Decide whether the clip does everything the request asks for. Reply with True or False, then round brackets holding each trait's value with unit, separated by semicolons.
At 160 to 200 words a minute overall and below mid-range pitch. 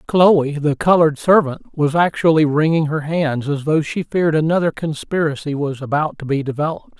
False (170 wpm; 155 Hz)